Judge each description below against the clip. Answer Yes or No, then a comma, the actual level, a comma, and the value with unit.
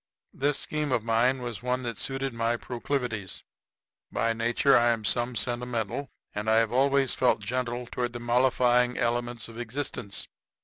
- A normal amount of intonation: No, narrow, 1.8 semitones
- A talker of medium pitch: No, low, 120 Hz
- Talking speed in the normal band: Yes, average, 150 wpm